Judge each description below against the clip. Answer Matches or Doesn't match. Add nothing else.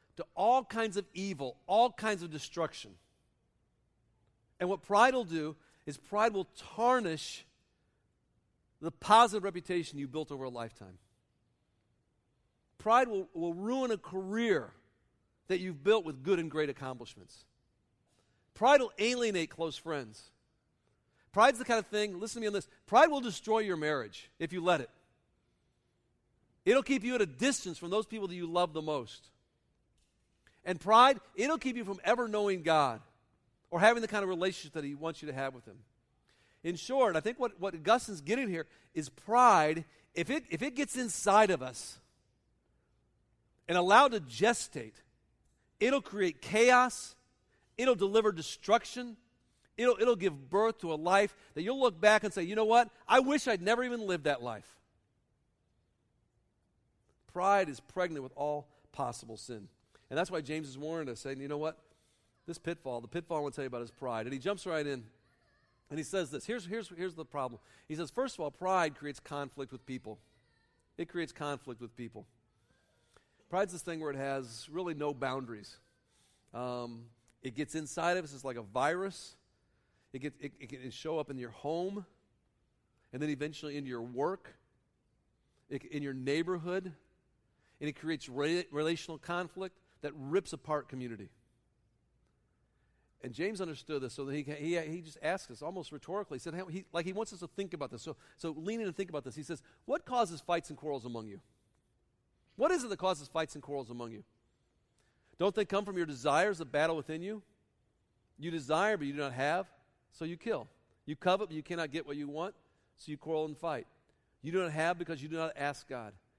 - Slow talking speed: Doesn't match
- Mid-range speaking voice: Matches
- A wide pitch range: Matches